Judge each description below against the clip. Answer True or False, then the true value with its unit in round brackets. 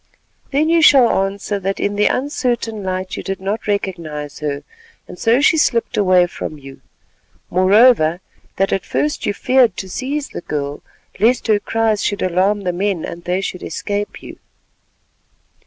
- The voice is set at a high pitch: True (200 Hz)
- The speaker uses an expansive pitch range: False (4.0 semitones)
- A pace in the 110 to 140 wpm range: False (165 wpm)